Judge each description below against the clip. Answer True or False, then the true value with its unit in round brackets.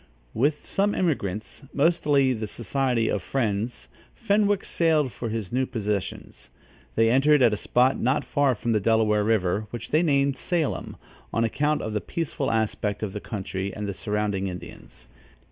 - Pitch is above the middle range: False (115 Hz)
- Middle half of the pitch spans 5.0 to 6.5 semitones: True (5.3 semitones)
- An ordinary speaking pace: True (165 wpm)